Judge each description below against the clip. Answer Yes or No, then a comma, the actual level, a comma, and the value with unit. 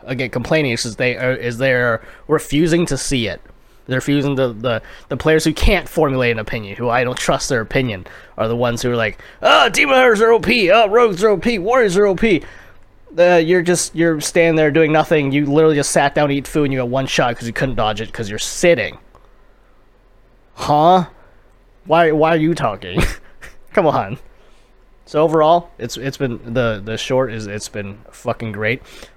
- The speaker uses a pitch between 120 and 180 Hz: Yes, low, 135 Hz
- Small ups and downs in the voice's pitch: No, wide, 5.5 semitones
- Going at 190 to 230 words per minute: Yes, average, 200 wpm